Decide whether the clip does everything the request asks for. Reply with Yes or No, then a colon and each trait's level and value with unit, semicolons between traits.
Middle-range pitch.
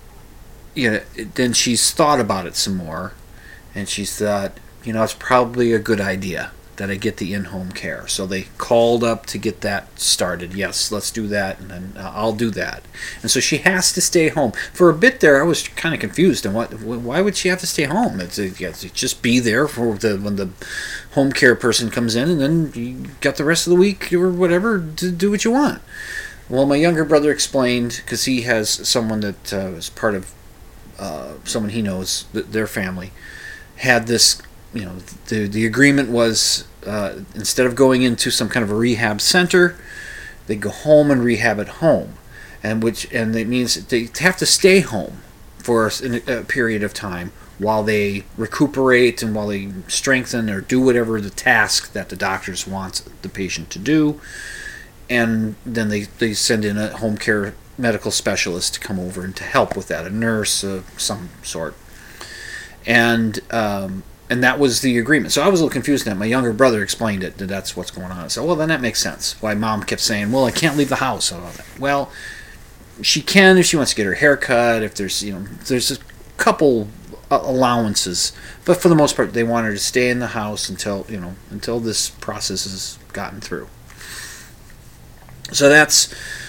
No: low, 115 Hz